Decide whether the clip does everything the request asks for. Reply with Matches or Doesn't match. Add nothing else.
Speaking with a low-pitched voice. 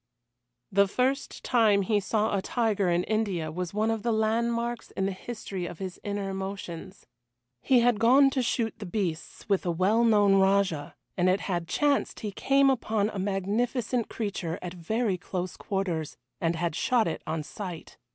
Doesn't match